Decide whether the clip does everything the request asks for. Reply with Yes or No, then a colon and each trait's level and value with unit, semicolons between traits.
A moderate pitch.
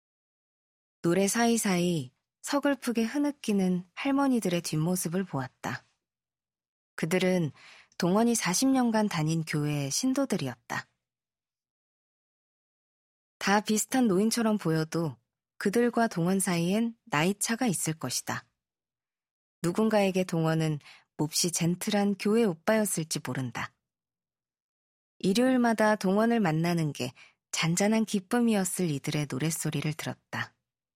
Yes: medium, 180 Hz